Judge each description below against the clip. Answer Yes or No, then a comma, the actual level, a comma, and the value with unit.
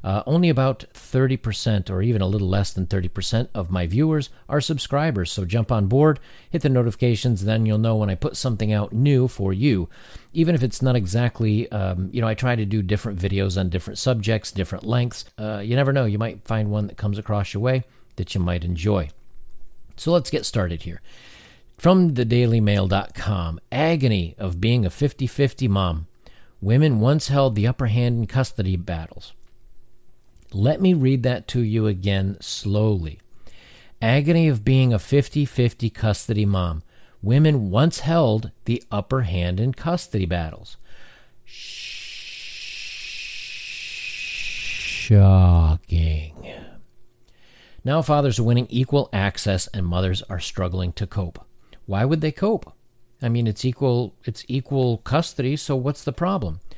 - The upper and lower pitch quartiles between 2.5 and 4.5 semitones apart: No, average, 5.2 semitones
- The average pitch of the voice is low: Yes, low, 110 Hz